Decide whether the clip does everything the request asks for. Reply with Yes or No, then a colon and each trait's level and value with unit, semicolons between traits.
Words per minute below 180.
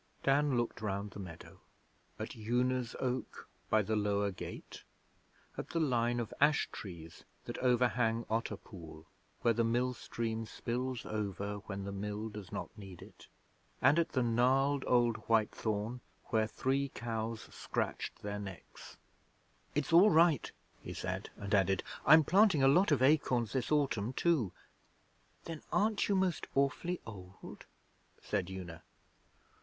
Yes: average, 145 wpm